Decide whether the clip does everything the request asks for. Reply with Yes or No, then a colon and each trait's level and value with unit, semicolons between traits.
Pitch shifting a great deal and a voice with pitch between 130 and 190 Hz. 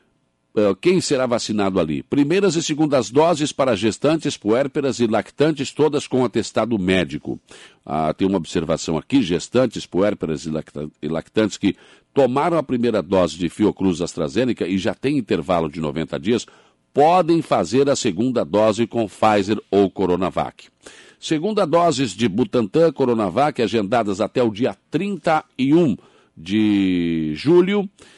No: wide, 7.8 semitones; low, 120 Hz